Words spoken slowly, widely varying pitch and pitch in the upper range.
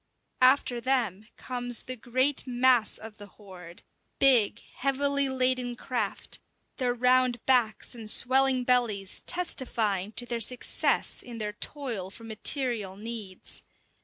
No: slow, 125 wpm; average, 3.1 semitones; high, 245 Hz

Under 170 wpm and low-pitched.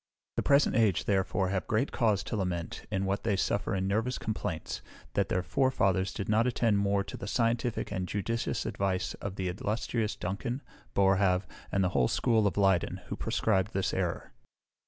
No: average, 175 wpm; low, 100 Hz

